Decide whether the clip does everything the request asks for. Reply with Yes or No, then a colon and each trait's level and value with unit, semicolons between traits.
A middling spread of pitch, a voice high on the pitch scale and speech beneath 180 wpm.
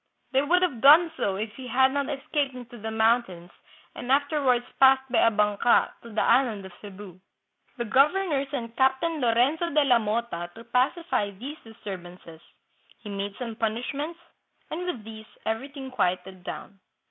Yes: average, 4.6 semitones; high, 240 Hz; average, 160 wpm